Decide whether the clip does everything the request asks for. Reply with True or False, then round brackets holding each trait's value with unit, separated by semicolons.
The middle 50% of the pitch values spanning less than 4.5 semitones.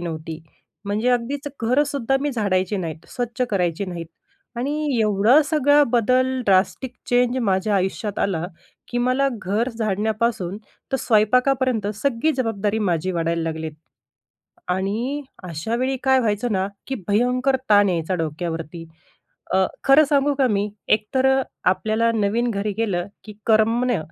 False (5.0 semitones)